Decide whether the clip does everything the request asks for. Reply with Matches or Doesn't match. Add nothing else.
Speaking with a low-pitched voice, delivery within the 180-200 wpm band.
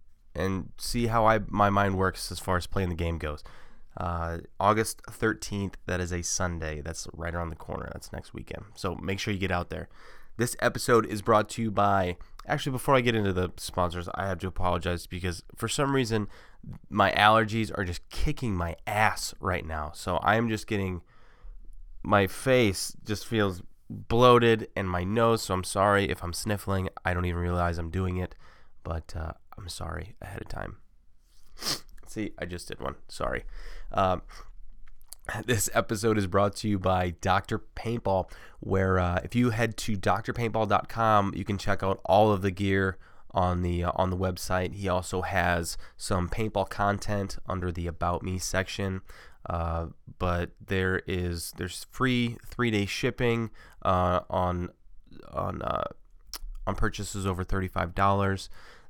Doesn't match